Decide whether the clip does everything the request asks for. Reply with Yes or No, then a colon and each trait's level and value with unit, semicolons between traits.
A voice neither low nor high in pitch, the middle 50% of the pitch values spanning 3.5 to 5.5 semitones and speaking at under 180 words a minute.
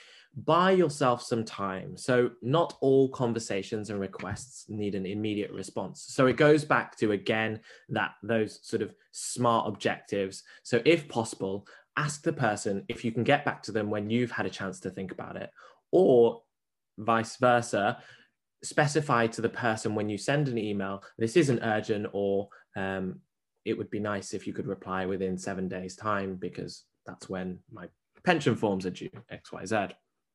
No: low, 110 Hz; average, 4.0 semitones; average, 170 wpm